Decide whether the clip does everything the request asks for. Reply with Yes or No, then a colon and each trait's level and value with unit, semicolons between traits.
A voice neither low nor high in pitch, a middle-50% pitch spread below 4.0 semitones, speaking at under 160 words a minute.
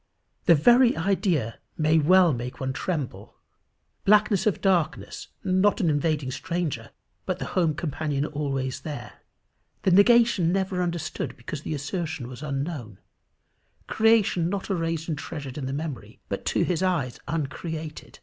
No: medium, 160 Hz; average, 4.5 semitones; average, 140 wpm